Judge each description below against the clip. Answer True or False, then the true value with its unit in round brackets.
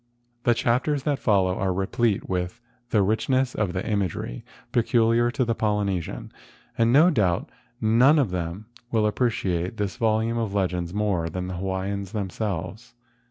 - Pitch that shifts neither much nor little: True (4.0 semitones)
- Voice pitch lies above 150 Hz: False (105 Hz)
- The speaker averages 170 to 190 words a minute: False (160 wpm)